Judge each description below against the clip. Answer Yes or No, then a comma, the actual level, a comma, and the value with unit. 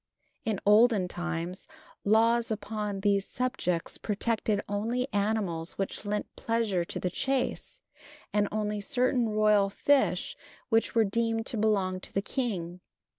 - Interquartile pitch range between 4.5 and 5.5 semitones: No, average, 2.7 semitones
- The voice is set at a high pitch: Yes, high, 210 Hz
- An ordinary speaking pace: No, slow, 130 wpm